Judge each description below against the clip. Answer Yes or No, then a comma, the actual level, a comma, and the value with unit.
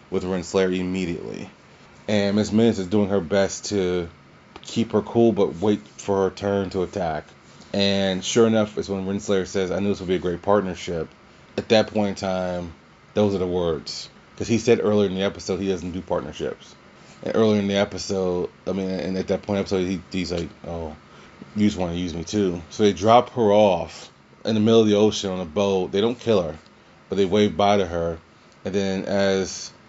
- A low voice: Yes, very low, 95 Hz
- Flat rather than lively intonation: Yes, narrow, 2.0 semitones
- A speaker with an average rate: No, fast, 215 wpm